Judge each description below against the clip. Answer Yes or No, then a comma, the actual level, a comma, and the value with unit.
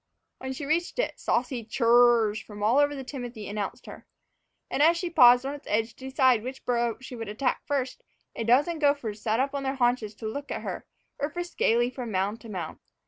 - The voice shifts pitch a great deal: No, average, 3.9 semitones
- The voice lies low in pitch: No, high, 245 Hz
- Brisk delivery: Yes, fast, 225 wpm